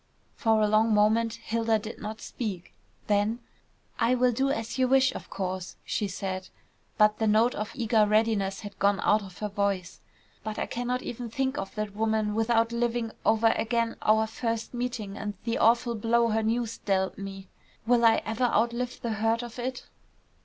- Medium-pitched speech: No, high, 225 Hz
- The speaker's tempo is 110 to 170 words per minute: No, average, 180 wpm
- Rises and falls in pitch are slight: Yes, narrow, 2.0 semitones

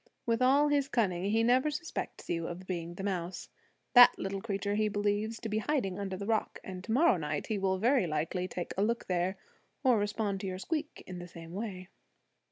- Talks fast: Yes, fast, 210 wpm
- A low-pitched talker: No, high, 200 Hz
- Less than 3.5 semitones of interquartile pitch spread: No, average, 4.0 semitones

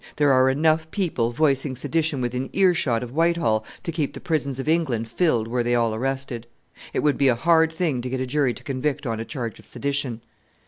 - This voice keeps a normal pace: No, fast, 215 wpm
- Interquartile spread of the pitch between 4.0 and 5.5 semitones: Yes, average, 4.5 semitones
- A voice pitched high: No, low, 135 Hz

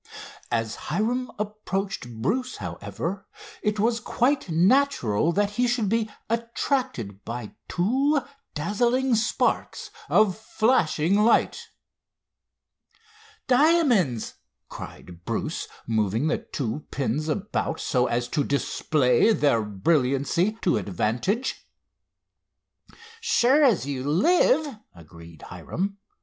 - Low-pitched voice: No, high, 190 Hz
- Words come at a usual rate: No, slow, 100 wpm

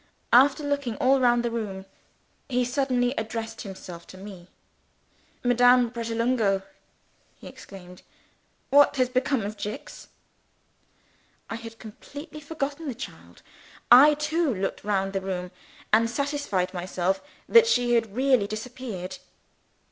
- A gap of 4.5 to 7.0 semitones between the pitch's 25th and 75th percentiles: Yes, average, 5.2 semitones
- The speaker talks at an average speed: No, slow, 125 wpm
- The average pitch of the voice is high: Yes, high, 235 Hz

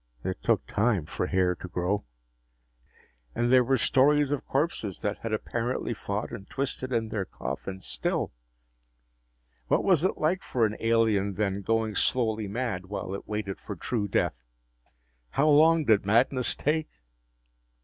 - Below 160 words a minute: Yes, average, 150 wpm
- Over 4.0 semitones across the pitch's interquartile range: Yes, average, 4.5 semitones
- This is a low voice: Yes, low, 115 Hz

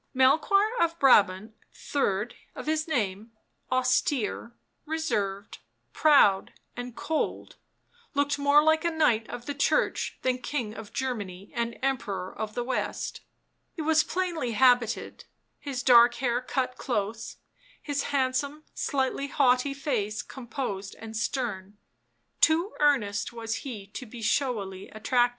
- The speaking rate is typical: No, slow, 130 wpm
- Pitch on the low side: No, very high, 250 Hz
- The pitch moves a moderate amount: Yes, average, 4.7 semitones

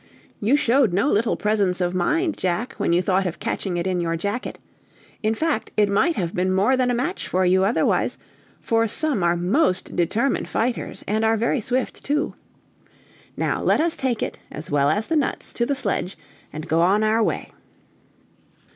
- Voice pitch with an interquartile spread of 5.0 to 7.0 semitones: Yes, wide, 5.5 semitones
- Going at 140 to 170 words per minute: No, average, 190 wpm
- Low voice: No, high, 210 Hz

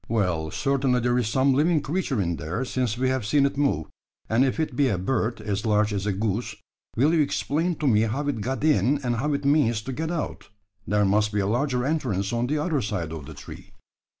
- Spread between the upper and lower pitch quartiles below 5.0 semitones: No, average, 5.3 semitones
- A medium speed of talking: No, fast, 230 wpm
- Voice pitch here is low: Yes, low, 125 Hz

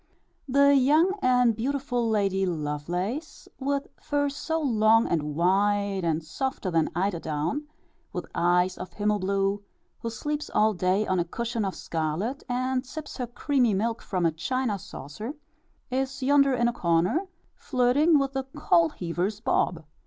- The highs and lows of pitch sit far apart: Yes, wide, 6.7 semitones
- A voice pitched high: Yes, high, 220 Hz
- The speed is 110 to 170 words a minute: Yes, average, 150 wpm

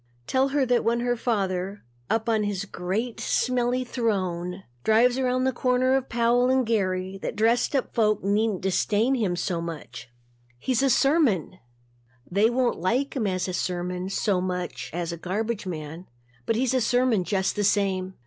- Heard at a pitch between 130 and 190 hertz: No, high, 215 Hz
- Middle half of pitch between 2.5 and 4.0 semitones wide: No, average, 4.9 semitones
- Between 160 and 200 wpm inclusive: Yes, average, 170 wpm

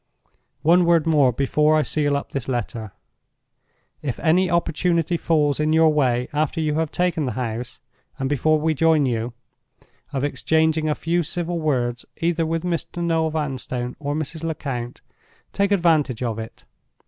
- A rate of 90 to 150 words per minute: No, average, 160 wpm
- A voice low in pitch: No, medium, 155 Hz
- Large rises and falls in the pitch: No, average, 3.7 semitones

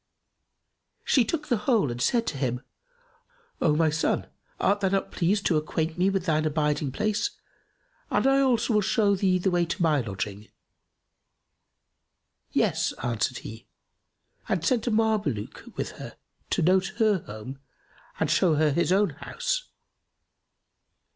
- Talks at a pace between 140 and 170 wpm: Yes, average, 150 wpm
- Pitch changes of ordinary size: No, wide, 6.1 semitones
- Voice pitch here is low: No, medium, 180 Hz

